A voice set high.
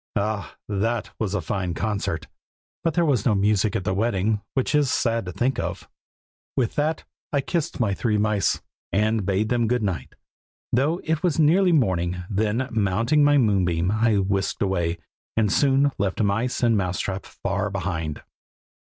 No: low, 105 Hz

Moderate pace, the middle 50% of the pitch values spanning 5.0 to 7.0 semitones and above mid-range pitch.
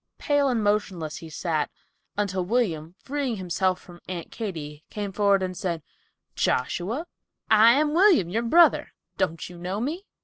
Yes: average, 150 wpm; wide, 5.5 semitones; high, 195 Hz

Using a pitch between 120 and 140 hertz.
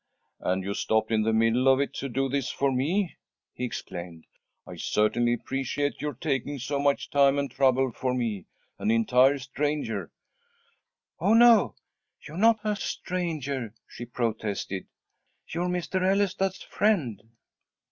Yes: low, 135 Hz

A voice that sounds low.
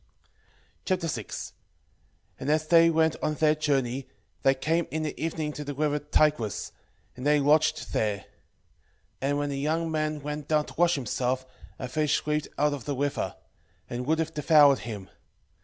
No: medium, 150 Hz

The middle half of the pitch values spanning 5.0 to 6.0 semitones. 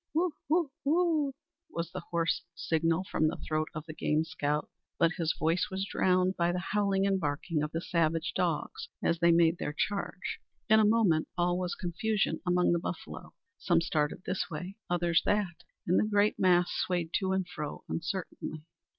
No: average, 2.8 semitones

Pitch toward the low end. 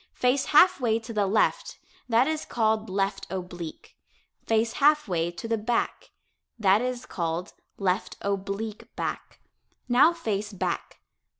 No: high, 220 Hz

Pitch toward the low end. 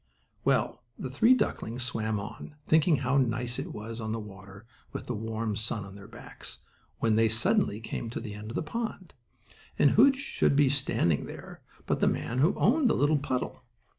Yes: low, 120 Hz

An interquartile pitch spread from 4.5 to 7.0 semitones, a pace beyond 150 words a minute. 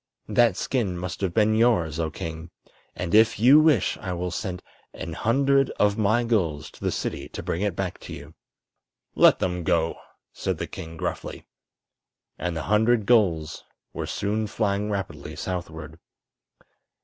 Yes: average, 4.9 semitones; average, 160 wpm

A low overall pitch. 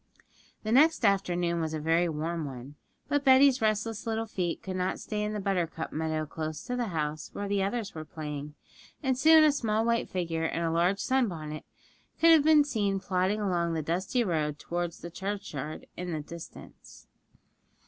No: medium, 185 Hz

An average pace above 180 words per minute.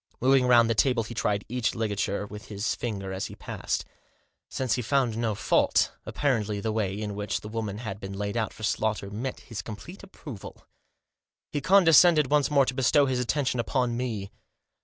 Yes: average, 190 wpm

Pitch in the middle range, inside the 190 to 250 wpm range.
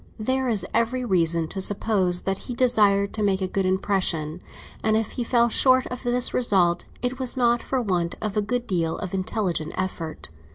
No: high, 205 Hz; average, 195 wpm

